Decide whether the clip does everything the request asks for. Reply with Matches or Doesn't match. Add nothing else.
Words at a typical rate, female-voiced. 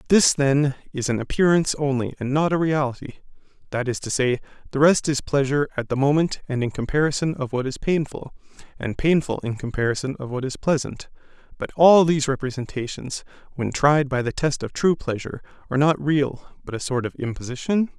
Doesn't match